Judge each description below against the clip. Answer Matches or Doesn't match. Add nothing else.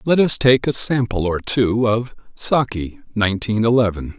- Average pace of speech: Matches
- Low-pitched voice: Matches